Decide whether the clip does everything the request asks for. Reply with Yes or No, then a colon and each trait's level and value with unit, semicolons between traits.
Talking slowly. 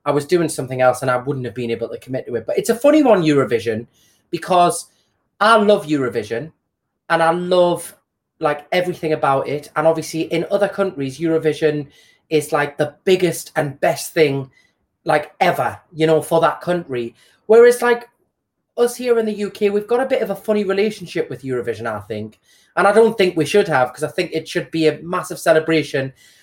No: average, 200 wpm